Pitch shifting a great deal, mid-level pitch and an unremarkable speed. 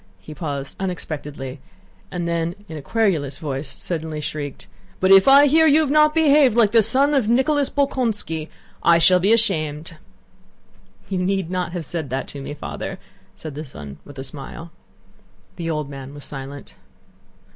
Yes: wide, 7.6 semitones; medium, 170 Hz; average, 170 wpm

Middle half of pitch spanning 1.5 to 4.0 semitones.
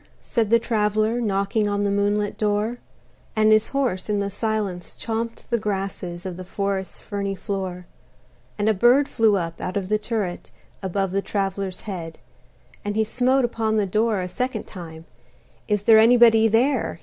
Yes: narrow, 2.4 semitones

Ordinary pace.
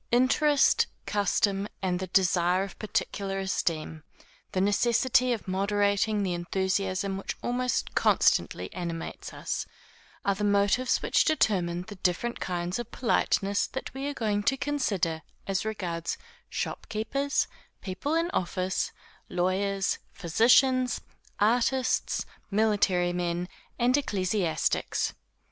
No: slow, 115 wpm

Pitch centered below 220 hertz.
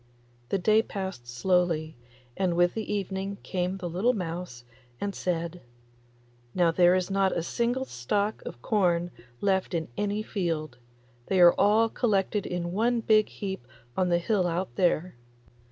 Yes: medium, 185 Hz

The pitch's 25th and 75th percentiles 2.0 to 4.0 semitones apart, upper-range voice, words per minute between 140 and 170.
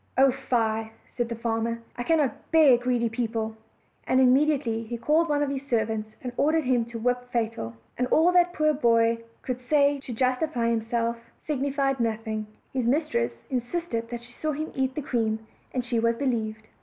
No: average, 3.4 semitones; high, 245 Hz; average, 190 wpm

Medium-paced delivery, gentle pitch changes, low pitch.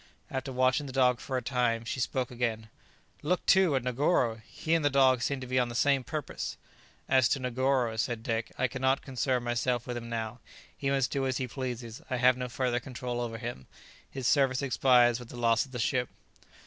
No: fast, 210 wpm; narrow, 1.8 semitones; low, 125 Hz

